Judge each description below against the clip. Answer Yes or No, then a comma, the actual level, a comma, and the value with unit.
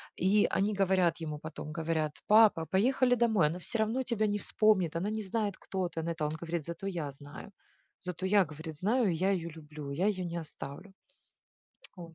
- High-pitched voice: No, medium, 180 Hz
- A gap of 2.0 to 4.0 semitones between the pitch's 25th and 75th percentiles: No, average, 4.4 semitones